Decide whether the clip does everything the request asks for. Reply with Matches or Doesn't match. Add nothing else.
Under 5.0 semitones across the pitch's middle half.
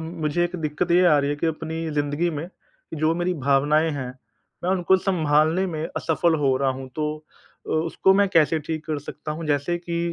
Matches